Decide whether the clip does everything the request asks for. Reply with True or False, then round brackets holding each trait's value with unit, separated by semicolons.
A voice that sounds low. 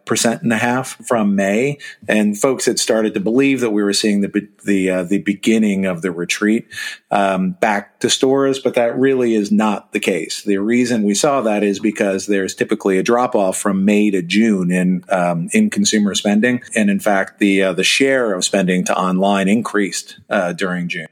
True (105 Hz)